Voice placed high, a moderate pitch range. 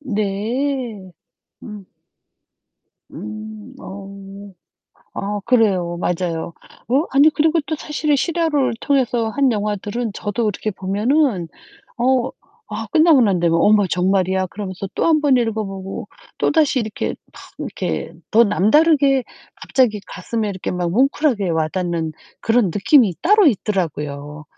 No: high, 215 Hz; wide, 5.9 semitones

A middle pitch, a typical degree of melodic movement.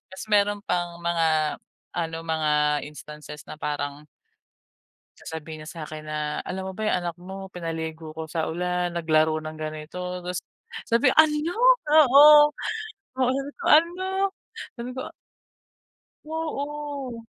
No: medium, 170 Hz; wide, 8.1 semitones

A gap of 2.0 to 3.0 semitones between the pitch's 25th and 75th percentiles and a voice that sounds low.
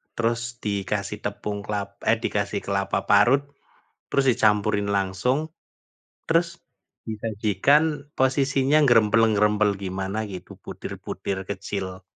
No: average, 3.4 semitones; low, 105 Hz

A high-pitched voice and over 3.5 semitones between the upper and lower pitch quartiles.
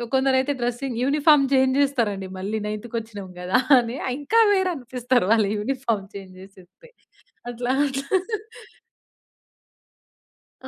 Yes: high, 245 Hz; average, 4.5 semitones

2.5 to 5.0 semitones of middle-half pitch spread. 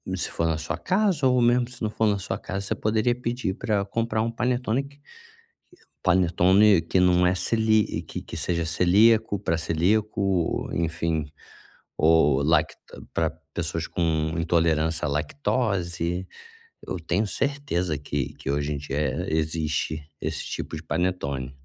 No: wide, 5.4 semitones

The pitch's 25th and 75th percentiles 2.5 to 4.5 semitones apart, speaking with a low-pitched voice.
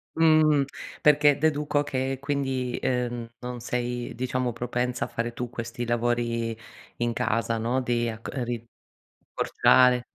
No: narrow, 2.0 semitones; low, 125 Hz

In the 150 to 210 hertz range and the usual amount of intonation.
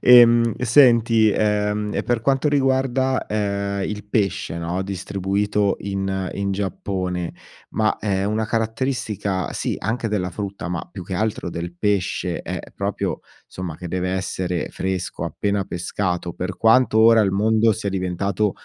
No: low, 100 Hz; average, 3.0 semitones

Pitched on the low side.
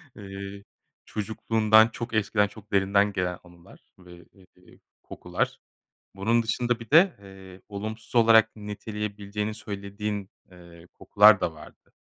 Yes: low, 105 Hz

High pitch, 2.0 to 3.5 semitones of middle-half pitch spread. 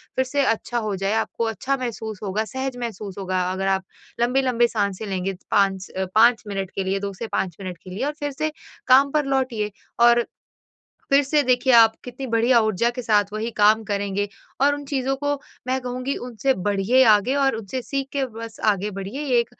No: high, 230 Hz; average, 4.5 semitones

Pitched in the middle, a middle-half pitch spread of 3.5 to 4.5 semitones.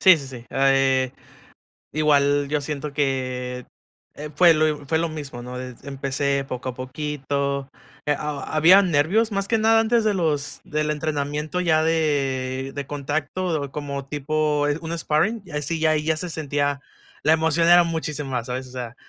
No: medium, 145 Hz; average, 2.7 semitones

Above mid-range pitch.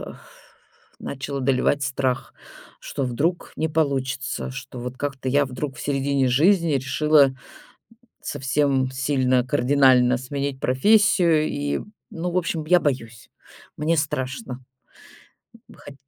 No: medium, 140 Hz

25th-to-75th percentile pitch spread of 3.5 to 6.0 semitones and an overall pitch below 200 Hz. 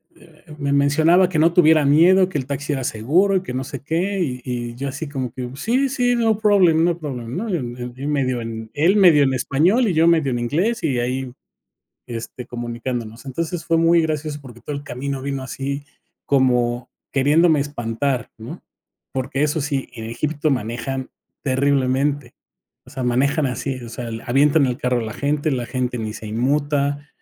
Yes: average, 4.1 semitones; medium, 140 Hz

